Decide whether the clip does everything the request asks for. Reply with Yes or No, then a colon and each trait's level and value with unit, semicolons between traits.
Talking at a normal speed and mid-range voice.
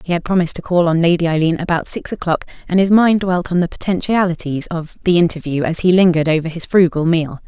No: fast, 225 wpm; medium, 170 Hz